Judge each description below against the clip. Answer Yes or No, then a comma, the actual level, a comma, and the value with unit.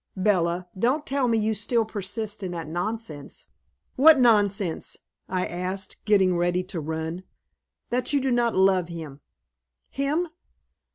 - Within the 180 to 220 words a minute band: No, slow, 135 wpm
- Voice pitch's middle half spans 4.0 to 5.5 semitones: Yes, average, 4.9 semitones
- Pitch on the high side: Yes, high, 195 Hz